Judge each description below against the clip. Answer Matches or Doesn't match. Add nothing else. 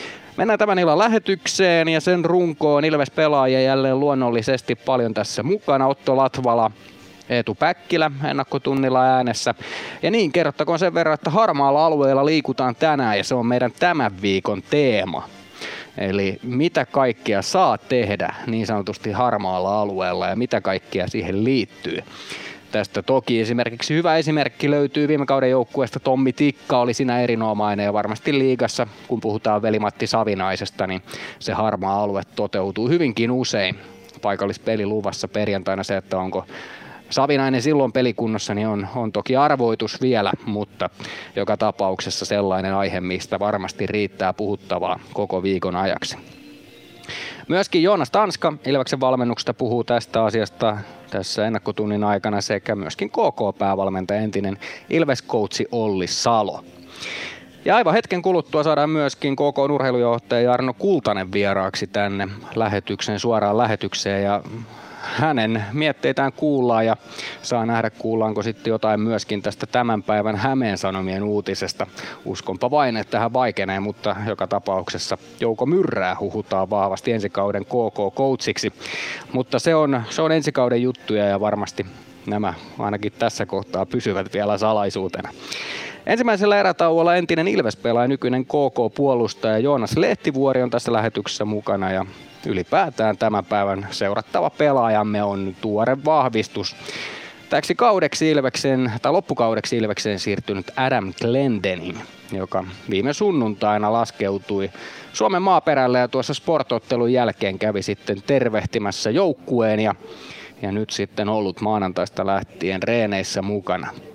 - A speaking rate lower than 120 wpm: Doesn't match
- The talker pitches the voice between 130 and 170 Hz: Doesn't match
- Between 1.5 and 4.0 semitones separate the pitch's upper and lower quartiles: Doesn't match